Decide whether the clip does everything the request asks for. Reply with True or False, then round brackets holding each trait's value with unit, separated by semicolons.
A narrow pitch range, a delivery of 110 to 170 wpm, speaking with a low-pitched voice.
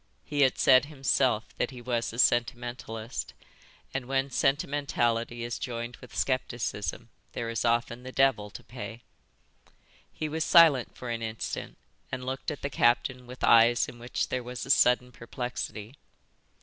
True (2.0 semitones; 155 wpm; 125 Hz)